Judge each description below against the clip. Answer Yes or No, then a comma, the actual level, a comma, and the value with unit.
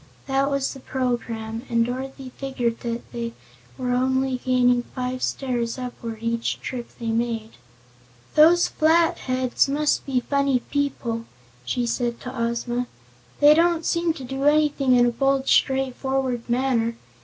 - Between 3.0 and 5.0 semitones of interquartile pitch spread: No, narrow, 2.4 semitones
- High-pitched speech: Yes, very high, 255 Hz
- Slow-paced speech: No, average, 145 wpm